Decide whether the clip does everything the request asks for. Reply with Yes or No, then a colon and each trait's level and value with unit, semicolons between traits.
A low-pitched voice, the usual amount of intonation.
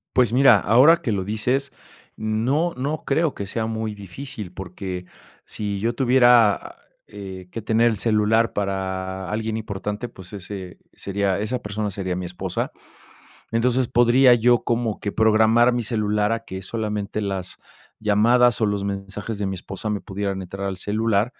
Yes: low, 105 Hz; average, 3.2 semitones